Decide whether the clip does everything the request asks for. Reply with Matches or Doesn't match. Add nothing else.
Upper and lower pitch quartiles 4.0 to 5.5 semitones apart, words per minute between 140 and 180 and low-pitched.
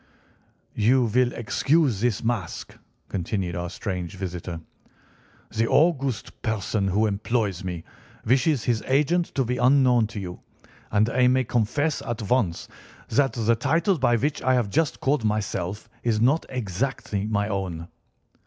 Matches